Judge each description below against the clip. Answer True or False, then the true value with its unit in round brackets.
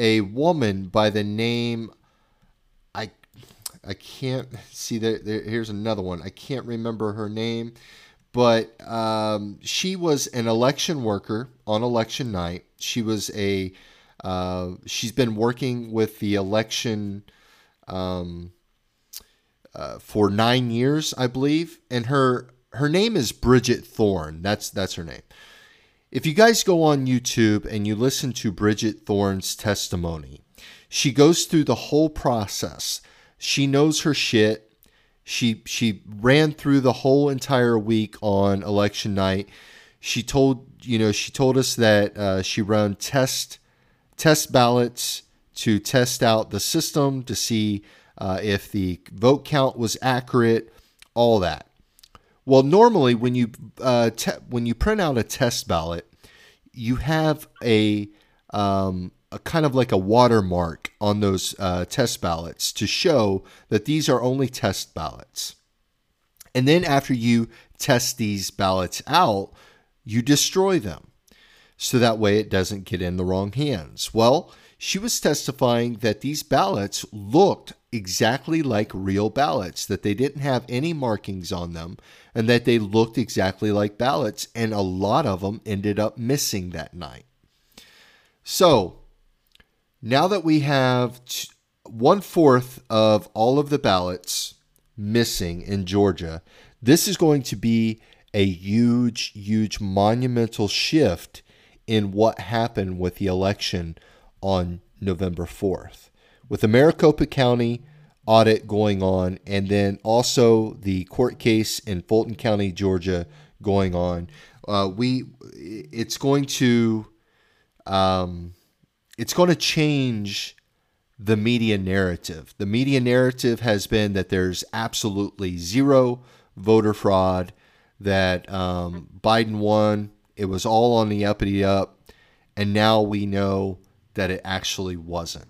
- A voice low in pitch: True (110 Hz)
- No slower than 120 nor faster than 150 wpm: True (135 wpm)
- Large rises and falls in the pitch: False (4.2 semitones)